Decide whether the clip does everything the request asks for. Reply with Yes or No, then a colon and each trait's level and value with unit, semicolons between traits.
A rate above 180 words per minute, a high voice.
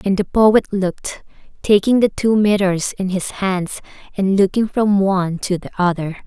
No: average, 165 wpm; high, 195 Hz